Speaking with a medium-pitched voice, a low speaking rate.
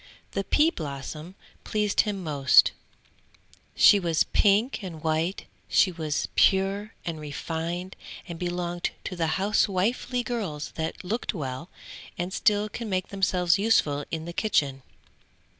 Yes: medium, 180 Hz; slow, 130 wpm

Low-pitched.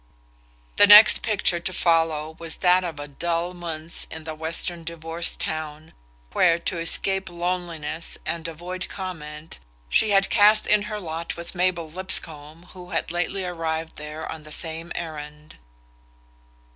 No: medium, 170 Hz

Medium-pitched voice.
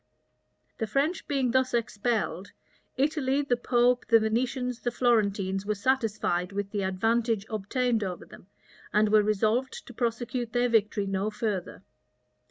No: high, 225 Hz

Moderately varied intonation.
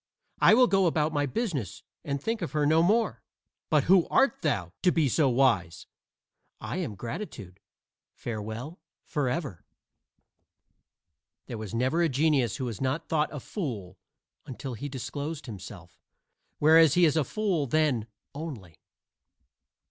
No: wide, 5.8 semitones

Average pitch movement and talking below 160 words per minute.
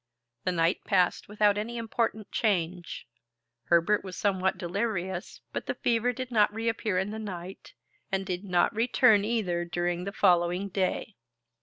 Yes: average, 3.6 semitones; average, 150 wpm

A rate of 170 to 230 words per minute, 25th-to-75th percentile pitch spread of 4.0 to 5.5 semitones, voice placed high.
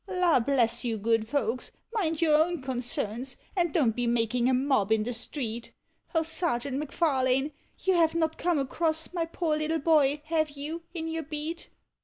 Yes: average, 175 wpm; average, 4.8 semitones; very high, 295 Hz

